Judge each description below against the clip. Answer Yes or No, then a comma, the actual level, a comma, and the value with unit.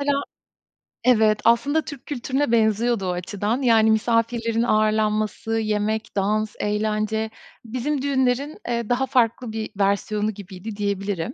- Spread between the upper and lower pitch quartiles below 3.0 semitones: Yes, narrow, 2.5 semitones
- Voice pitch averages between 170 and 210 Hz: No, high, 220 Hz